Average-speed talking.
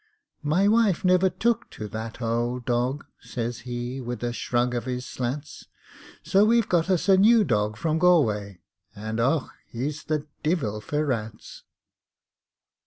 Yes: average, 150 wpm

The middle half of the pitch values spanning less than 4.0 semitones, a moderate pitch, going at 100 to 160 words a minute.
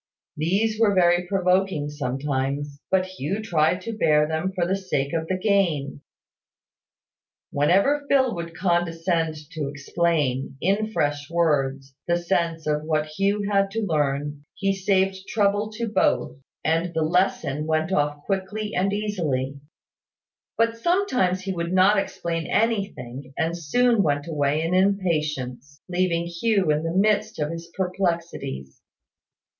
No: average, 4.6 semitones; medium, 170 Hz; average, 140 wpm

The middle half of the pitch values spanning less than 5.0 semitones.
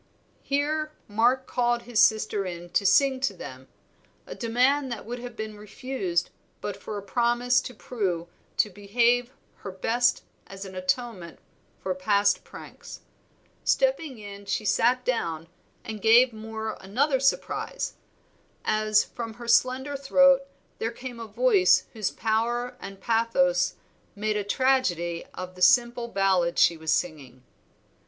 Yes: average, 4.2 semitones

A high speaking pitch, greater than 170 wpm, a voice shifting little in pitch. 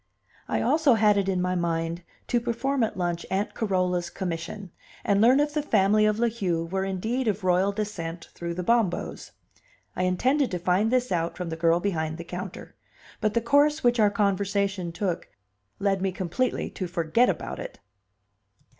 No: high, 195 Hz; average, 180 wpm; average, 4.2 semitones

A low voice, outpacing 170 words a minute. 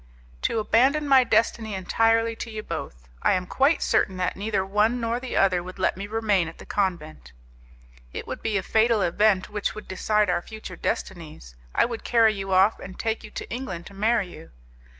No: high, 210 Hz; average, 200 wpm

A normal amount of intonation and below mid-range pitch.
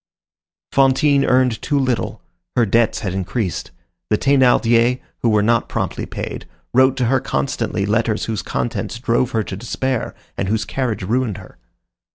Yes: average, 3.1 semitones; low, 120 Hz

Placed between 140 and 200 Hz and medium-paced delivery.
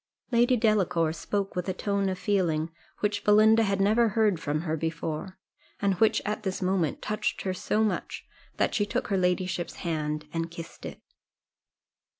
Yes: high, 190 Hz; average, 165 wpm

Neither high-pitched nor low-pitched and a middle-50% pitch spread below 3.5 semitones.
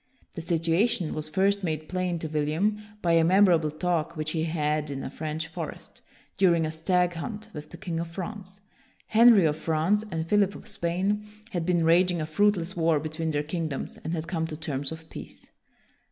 Yes: medium, 165 Hz; average, 2.8 semitones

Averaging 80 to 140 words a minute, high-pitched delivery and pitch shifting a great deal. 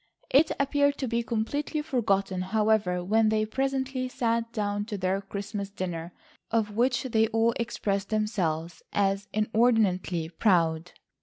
No: slow, 135 wpm; high, 215 Hz; average, 3.3 semitones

